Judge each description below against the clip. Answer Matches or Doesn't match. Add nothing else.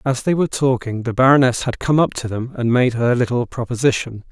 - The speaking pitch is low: Matches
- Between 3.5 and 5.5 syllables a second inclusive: Doesn't match